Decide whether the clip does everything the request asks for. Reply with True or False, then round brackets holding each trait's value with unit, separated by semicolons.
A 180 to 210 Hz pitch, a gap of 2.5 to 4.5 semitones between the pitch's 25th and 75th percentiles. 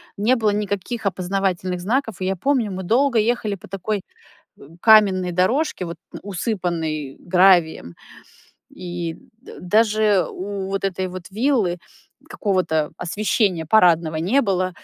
True (190 Hz; 3.4 semitones)